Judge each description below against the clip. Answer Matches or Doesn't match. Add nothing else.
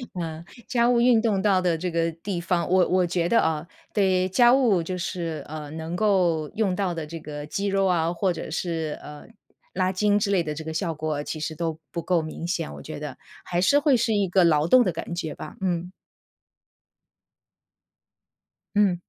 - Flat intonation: Doesn't match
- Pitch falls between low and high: Matches